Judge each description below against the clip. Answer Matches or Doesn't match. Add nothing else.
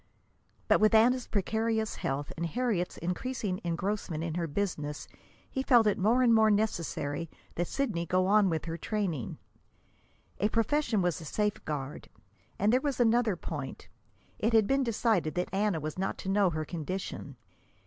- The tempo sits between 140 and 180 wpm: Matches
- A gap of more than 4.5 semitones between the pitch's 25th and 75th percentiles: Matches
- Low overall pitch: Doesn't match